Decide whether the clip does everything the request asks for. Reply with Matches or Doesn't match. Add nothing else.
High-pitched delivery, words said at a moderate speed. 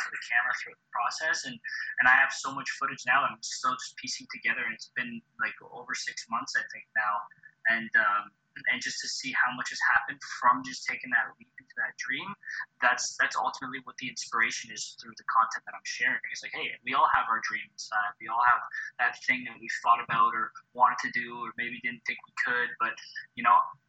Doesn't match